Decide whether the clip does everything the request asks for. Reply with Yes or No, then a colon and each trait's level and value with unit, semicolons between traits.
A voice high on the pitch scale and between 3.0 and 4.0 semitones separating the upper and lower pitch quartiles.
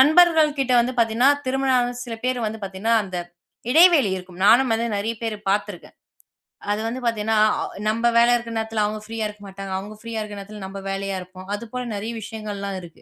Yes: high, 220 Hz; average, 3.3 semitones